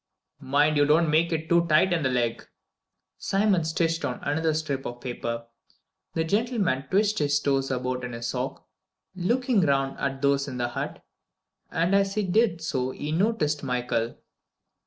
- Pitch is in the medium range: Yes, medium, 150 Hz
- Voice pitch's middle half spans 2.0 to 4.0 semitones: No, average, 4.9 semitones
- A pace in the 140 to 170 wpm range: Yes, average, 165 wpm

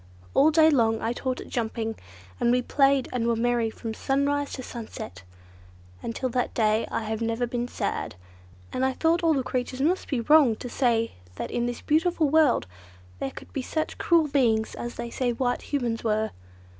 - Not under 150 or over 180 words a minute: No, average, 190 wpm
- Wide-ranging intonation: No, average, 3.5 semitones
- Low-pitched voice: No, high, 245 Hz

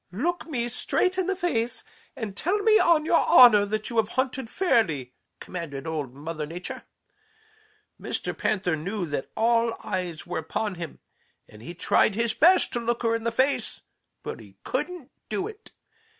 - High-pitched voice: Yes, high, 225 Hz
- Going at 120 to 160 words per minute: No, average, 170 wpm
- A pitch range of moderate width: No, wide, 8.0 semitones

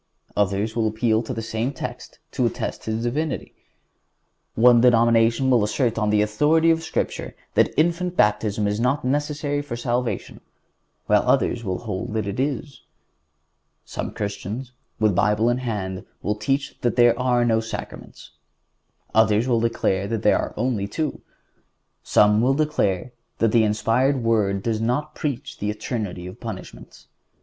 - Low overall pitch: Yes, low, 115 Hz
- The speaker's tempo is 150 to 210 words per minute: Yes, average, 155 wpm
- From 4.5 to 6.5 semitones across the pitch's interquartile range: No, average, 3.5 semitones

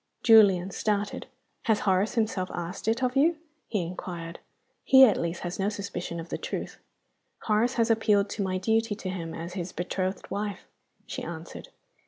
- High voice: Yes, high, 200 Hz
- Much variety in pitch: No, average, 3.6 semitones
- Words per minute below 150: No, average, 170 wpm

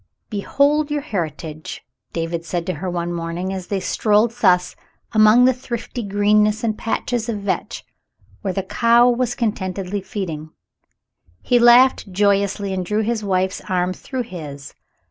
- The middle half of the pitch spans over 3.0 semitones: Yes, average, 4.4 semitones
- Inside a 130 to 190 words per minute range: Yes, average, 155 wpm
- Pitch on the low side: No, high, 200 Hz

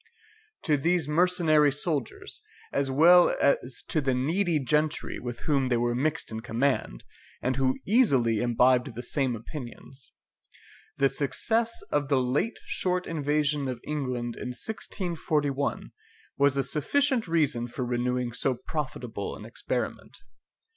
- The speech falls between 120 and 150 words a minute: Yes, slow, 135 wpm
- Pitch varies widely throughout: No, average, 3.8 semitones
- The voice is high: No, medium, 140 Hz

